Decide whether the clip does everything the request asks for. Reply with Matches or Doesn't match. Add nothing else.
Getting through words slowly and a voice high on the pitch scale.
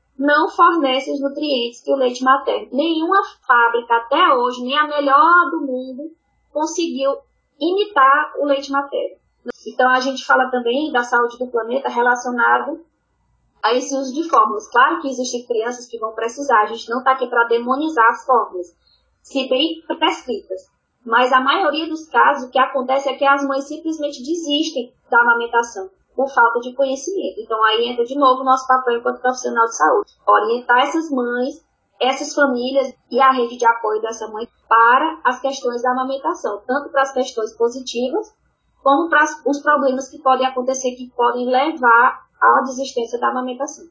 Doesn't match